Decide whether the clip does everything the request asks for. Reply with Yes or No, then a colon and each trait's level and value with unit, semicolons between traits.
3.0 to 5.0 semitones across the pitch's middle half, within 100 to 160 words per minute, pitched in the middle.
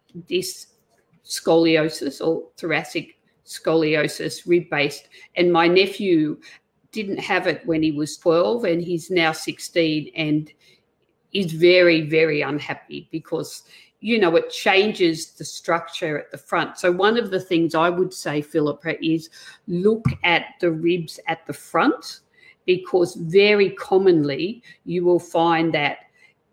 No: narrow, 2.6 semitones; slow, 135 wpm; medium, 170 Hz